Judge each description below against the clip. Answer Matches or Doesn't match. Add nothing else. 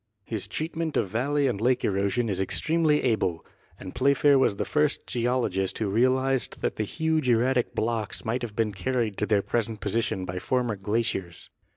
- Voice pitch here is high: Doesn't match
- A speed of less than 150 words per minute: Doesn't match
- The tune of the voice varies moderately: Matches